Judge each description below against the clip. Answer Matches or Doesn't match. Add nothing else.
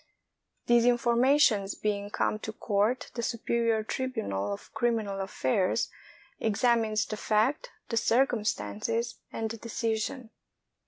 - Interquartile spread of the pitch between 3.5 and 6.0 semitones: Doesn't match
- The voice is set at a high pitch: Matches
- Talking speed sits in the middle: Doesn't match